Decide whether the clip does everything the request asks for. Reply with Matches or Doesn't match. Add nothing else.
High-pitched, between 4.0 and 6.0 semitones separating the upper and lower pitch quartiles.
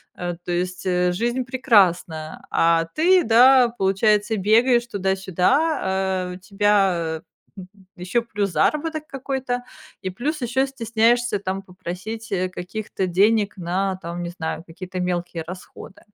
Matches